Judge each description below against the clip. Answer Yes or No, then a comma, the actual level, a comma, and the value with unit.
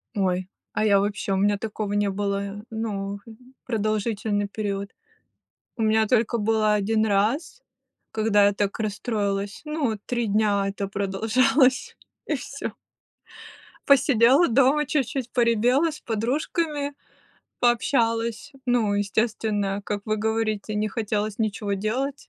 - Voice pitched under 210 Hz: No, high, 215 Hz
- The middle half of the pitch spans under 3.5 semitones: Yes, average, 2.8 semitones